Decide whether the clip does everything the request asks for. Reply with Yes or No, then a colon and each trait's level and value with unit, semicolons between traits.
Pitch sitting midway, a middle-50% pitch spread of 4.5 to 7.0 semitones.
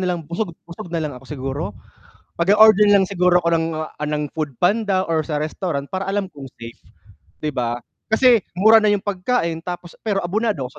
Yes: medium, 175 Hz; average, 5.1 semitones